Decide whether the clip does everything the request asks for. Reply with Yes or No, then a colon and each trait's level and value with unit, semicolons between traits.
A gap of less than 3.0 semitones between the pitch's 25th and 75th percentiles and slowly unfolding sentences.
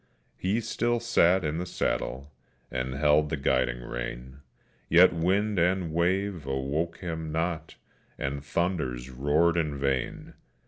No: average, 4.6 semitones; slow, 130 wpm